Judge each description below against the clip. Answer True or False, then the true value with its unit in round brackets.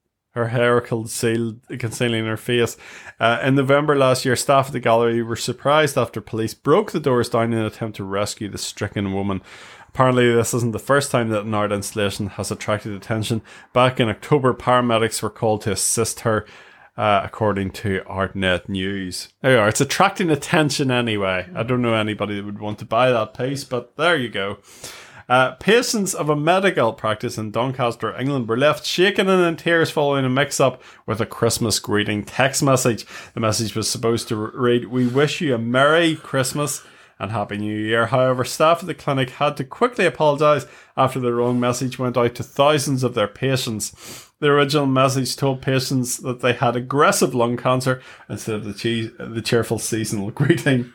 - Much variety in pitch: False (3.8 semitones)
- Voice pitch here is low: True (120 Hz)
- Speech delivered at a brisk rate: False (185 wpm)